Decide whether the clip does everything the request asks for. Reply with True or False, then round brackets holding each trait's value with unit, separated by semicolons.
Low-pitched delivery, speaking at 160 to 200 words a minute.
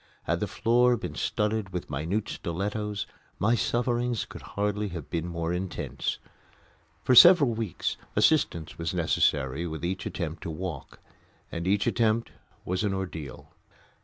False (95 Hz; 140 wpm)